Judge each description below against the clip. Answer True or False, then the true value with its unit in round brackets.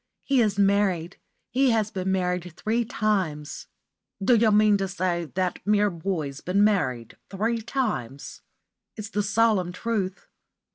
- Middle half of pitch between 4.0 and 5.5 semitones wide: False (3.1 semitones)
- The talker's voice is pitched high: True (200 Hz)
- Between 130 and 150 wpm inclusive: True (140 wpm)